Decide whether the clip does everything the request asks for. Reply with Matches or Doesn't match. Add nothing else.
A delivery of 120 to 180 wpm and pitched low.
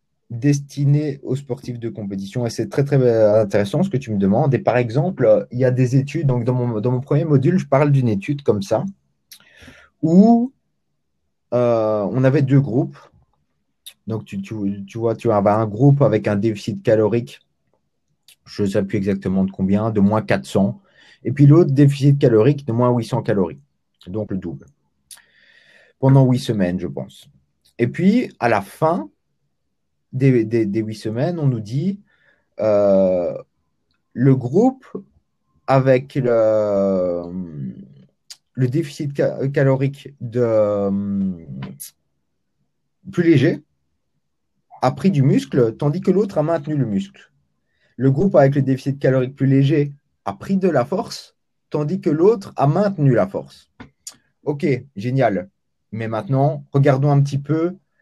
Matches